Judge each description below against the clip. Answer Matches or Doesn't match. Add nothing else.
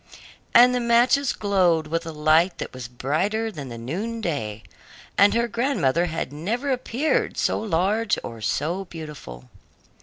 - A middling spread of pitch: Doesn't match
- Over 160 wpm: Doesn't match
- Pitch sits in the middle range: Matches